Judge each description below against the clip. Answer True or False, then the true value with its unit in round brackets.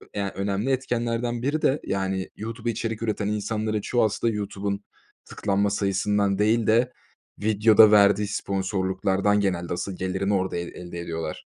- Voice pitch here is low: True (105 Hz)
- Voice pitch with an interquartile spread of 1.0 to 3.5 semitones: True (2.4 semitones)